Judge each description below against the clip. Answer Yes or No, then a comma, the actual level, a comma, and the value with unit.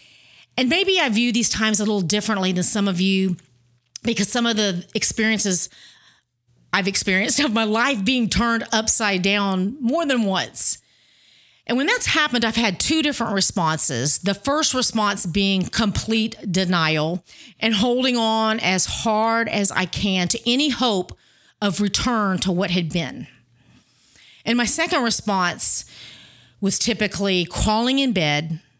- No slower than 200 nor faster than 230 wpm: No, average, 150 wpm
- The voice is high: Yes, high, 210 Hz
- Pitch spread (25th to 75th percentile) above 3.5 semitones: Yes, average, 3.9 semitones